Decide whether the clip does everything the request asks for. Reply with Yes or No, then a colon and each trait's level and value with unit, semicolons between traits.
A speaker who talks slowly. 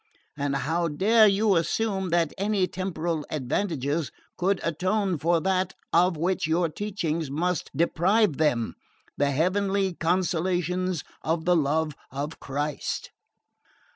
Yes: slow, 120 wpm